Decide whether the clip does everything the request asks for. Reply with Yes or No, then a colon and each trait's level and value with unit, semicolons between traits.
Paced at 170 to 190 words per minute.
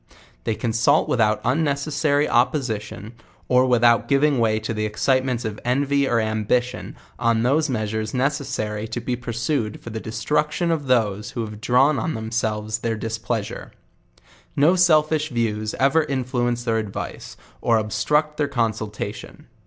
No: average, 145 wpm